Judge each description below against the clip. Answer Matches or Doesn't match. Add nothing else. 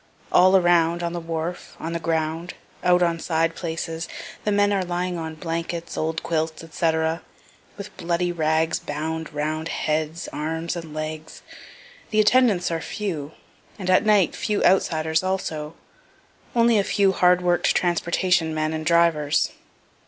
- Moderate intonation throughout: Doesn't match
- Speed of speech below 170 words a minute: Matches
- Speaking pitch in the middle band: Matches